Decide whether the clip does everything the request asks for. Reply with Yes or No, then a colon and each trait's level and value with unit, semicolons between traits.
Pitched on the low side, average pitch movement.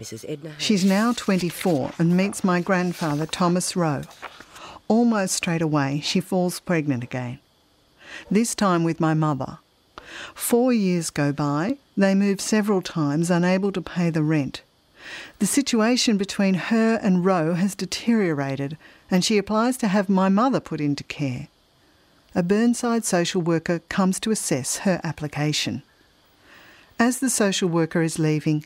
No: medium, 180 Hz; average, 4.5 semitones